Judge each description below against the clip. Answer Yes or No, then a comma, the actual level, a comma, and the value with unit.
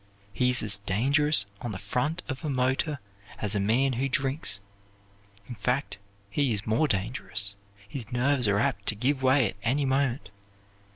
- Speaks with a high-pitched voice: No, low, 125 Hz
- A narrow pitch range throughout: No, average, 4.9 semitones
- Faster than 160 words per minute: Yes, average, 170 wpm